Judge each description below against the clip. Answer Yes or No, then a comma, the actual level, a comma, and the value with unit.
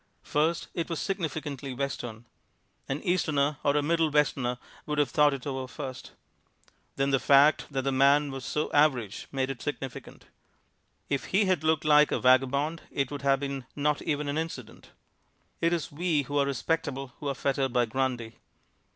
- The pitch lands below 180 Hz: Yes, medium, 140 Hz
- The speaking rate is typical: Yes, average, 175 wpm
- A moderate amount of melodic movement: No, narrow, 2.2 semitones